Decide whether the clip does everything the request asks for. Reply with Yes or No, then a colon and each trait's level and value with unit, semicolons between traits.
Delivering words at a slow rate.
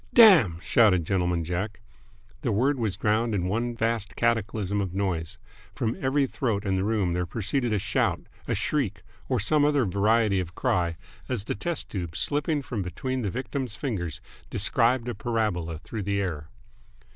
No: average, 170 wpm